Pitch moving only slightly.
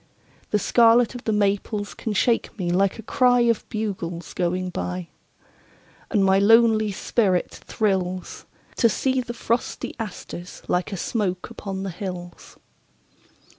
No: average, 3.8 semitones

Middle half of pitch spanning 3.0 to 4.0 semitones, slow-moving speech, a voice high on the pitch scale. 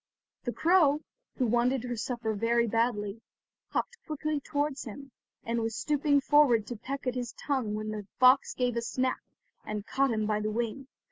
No: average, 3.7 semitones; average, 180 wpm; high, 245 Hz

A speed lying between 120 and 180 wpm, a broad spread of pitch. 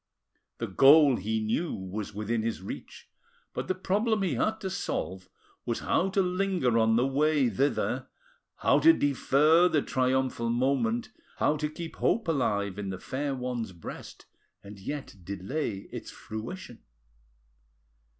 Yes: average, 145 wpm; wide, 6.4 semitones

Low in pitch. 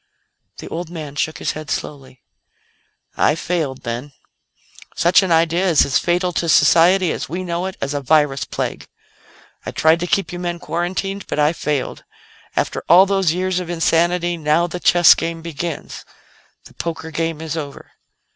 No: medium, 170 Hz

